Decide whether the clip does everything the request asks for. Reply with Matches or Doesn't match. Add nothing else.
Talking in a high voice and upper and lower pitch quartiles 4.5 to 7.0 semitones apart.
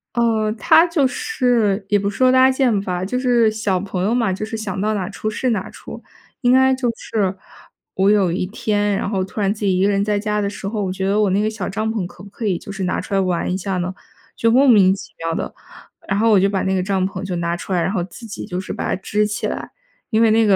Doesn't match